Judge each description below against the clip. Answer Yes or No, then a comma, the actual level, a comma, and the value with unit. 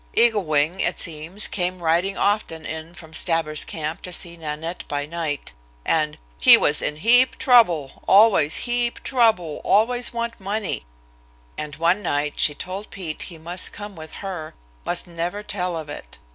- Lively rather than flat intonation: No, average, 4.6 semitones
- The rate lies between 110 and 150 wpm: No, average, 160 wpm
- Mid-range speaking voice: Yes, medium, 170 Hz